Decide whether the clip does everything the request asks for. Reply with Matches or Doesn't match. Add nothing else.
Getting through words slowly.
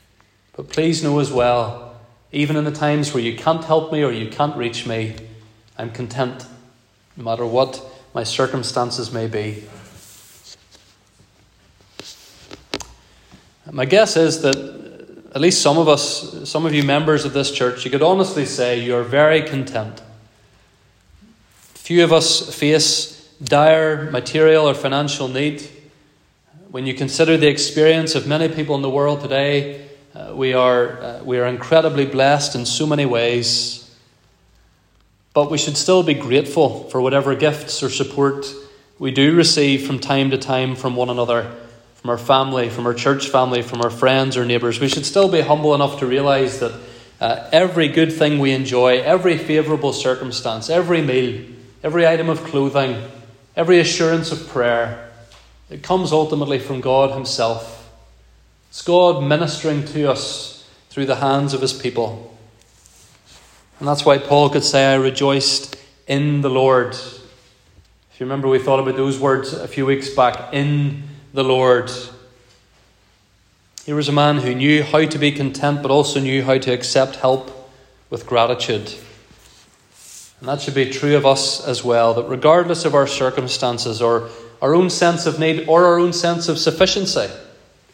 Doesn't match